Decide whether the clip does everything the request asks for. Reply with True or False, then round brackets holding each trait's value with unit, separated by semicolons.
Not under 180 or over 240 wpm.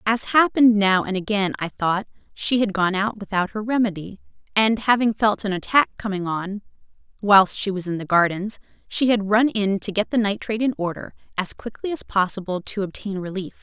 True (195 wpm)